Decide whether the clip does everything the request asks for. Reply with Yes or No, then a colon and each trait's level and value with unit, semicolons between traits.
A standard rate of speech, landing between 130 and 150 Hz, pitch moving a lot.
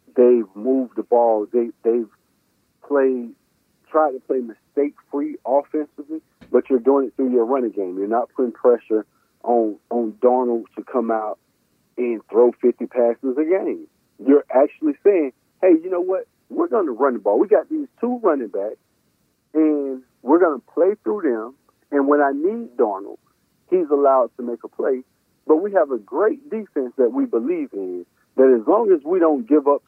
Yes: average, 185 wpm; medium, 140 Hz; wide, 7.4 semitones